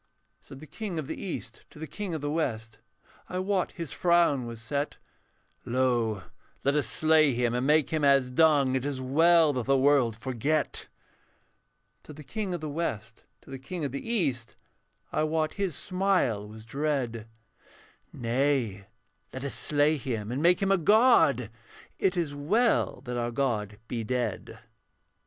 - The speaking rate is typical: Yes, average, 170 wpm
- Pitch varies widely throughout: No, average, 4.7 semitones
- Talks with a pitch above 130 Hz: Yes, medium, 140 Hz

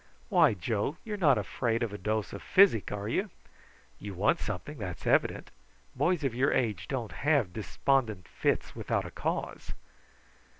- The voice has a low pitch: Yes, low, 115 Hz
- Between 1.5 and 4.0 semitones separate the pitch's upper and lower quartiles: No, wide, 5.5 semitones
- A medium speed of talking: Yes, average, 160 wpm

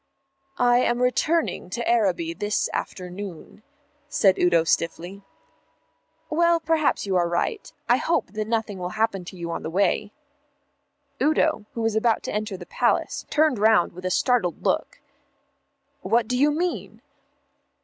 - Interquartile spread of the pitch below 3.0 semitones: No, average, 5.3 semitones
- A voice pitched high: Yes, high, 215 Hz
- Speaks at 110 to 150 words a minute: Yes, average, 145 wpm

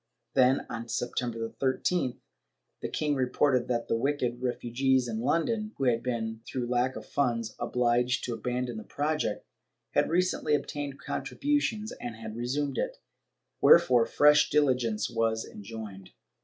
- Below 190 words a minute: Yes, average, 140 wpm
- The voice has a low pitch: Yes, low, 125 Hz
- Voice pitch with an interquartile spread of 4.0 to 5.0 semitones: No, average, 3.6 semitones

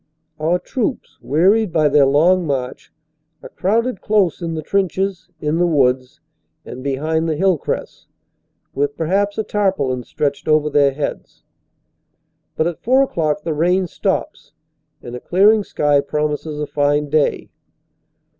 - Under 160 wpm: Yes, average, 145 wpm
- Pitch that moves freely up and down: No, average, 4.4 semitones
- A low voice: No, medium, 155 Hz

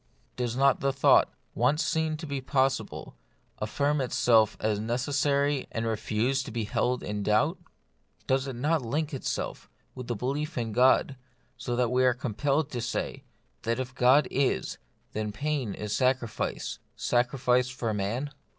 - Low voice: Yes, low, 125 Hz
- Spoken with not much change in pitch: No, average, 3.1 semitones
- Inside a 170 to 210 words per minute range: No, average, 160 wpm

